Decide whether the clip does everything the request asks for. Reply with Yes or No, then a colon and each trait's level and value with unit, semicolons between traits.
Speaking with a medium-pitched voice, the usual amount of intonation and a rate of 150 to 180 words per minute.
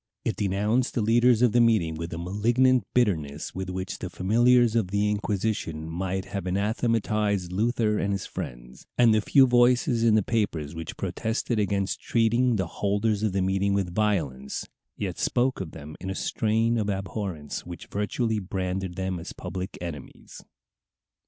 No: low, 100 Hz; average, 3.7 semitones; average, 165 wpm